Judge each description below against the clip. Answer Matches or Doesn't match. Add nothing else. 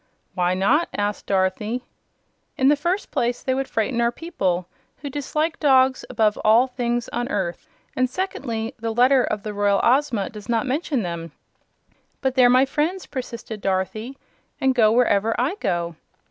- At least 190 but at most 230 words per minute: Doesn't match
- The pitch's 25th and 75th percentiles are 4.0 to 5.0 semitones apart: Matches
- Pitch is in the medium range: Doesn't match